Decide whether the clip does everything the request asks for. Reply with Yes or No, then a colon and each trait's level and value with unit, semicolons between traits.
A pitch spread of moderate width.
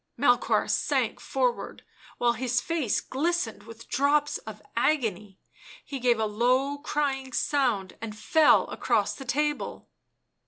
Yes: average, 4.4 semitones